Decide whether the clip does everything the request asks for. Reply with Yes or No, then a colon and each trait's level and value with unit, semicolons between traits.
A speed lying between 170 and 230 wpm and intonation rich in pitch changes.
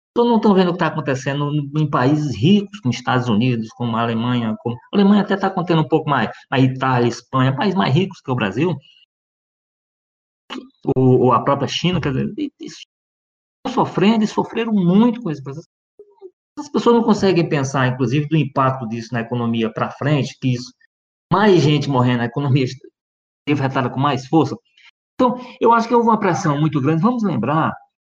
Yes: average, 180 wpm; wide, 7.5 semitones